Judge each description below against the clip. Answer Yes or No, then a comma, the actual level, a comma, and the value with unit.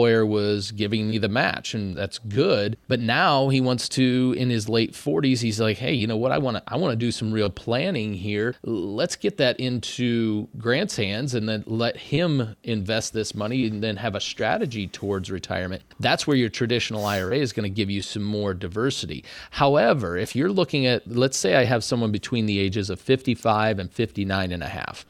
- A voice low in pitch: Yes, low, 110 Hz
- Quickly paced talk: Yes, fast, 210 wpm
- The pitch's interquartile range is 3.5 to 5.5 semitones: No, average, 3.0 semitones